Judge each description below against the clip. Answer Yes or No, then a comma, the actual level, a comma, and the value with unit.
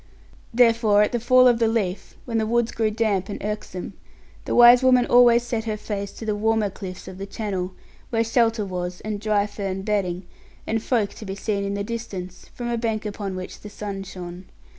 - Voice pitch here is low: No, high, 210 Hz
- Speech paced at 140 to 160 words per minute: No, fast, 205 wpm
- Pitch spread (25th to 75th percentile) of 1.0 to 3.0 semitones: Yes, average, 2.7 semitones